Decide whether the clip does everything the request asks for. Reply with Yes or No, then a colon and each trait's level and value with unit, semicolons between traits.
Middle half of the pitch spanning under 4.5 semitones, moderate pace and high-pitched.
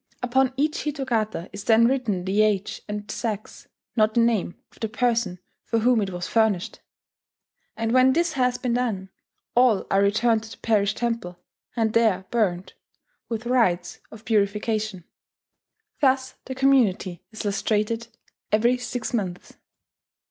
Yes: average, 3.3 semitones; average, 145 wpm; high, 225 Hz